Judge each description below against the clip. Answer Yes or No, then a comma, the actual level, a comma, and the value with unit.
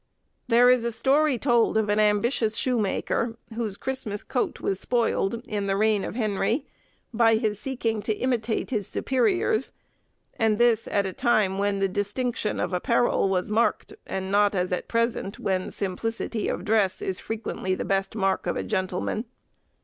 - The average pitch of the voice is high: Yes, high, 220 Hz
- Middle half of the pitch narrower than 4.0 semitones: Yes, average, 3.2 semitones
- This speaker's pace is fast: No, average, 165 wpm